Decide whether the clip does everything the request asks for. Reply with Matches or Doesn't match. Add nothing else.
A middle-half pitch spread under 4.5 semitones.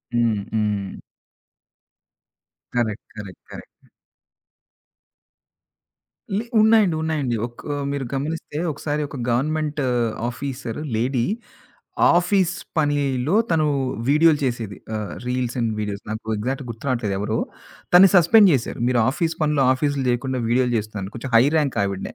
Doesn't match